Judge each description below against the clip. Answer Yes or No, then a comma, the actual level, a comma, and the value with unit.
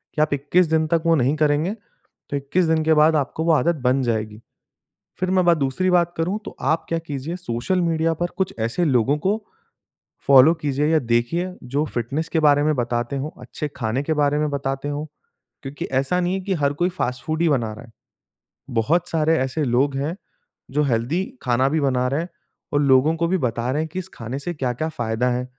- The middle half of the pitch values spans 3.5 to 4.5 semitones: Yes, average, 4.1 semitones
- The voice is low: No, medium, 150 Hz